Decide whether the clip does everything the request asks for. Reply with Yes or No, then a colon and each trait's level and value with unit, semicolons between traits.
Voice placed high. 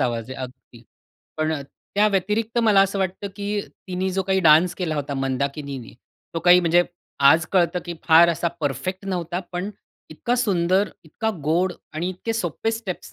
No: medium, 175 Hz